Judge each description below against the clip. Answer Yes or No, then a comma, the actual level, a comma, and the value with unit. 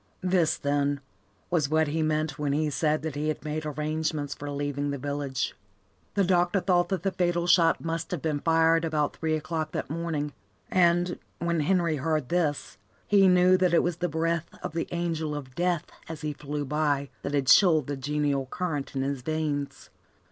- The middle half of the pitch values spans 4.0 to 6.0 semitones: No, average, 2.8 semitones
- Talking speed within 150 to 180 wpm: No, average, 190 wpm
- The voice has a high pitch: No, medium, 155 Hz